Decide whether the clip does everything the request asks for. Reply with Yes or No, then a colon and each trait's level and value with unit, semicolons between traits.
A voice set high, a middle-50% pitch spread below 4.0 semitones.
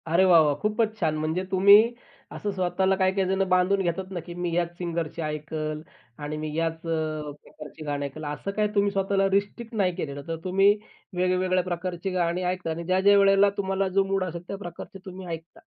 No: medium, 180 Hz; average, 2.9 semitones